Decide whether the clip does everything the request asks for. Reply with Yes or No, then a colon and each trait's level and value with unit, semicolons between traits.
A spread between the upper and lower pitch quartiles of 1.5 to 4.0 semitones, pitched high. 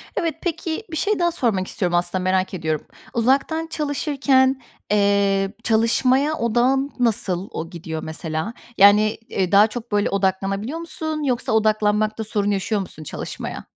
No: wide, 5.6 semitones; high, 215 Hz